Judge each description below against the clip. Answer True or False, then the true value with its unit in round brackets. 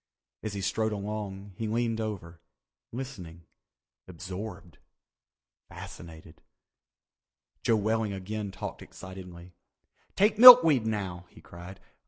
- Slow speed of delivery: True (95 wpm)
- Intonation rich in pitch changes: False (3.7 semitones)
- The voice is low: True (100 Hz)